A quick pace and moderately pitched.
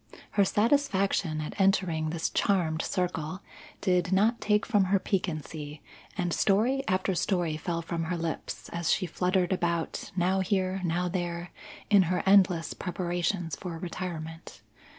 No: average, 140 wpm; medium, 180 Hz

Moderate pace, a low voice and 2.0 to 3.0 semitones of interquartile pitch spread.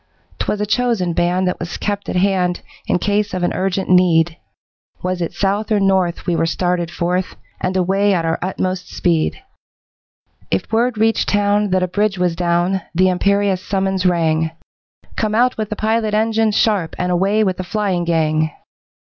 No: average, 175 wpm; medium, 185 Hz; average, 2.7 semitones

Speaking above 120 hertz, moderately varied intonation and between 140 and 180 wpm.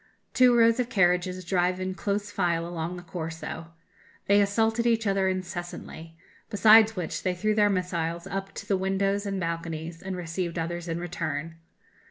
Yes: medium, 185 Hz; average, 3.1 semitones; average, 165 wpm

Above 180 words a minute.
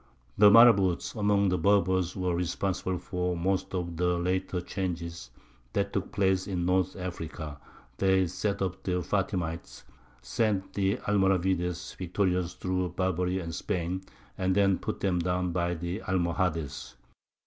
No: slow, 135 wpm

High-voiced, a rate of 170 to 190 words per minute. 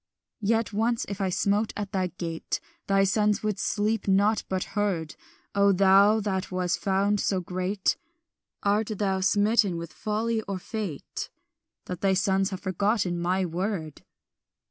No: high, 195 Hz; average, 145 wpm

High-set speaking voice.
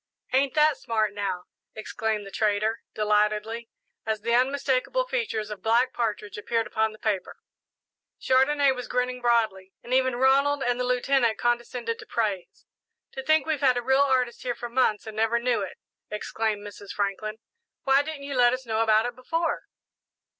Yes: high, 235 Hz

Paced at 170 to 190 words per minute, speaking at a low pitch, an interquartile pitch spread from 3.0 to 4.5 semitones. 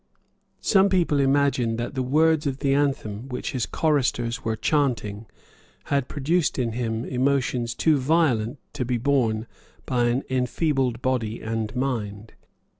No: average, 140 wpm; low, 130 Hz; average, 3.4 semitones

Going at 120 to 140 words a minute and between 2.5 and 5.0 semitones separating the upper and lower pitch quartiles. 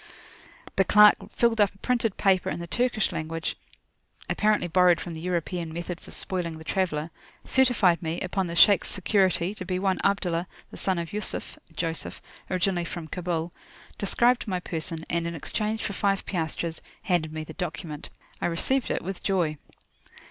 No: average, 170 wpm; average, 3.0 semitones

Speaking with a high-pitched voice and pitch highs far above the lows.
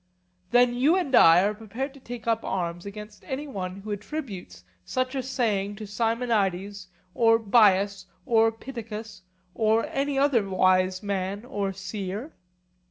No: high, 215 Hz; average, 3.9 semitones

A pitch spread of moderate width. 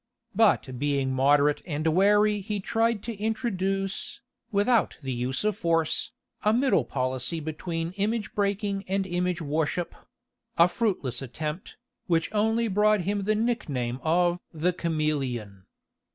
No: wide, 5.8 semitones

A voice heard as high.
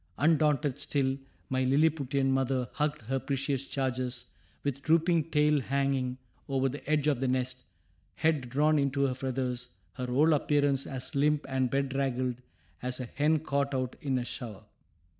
No: low, 135 Hz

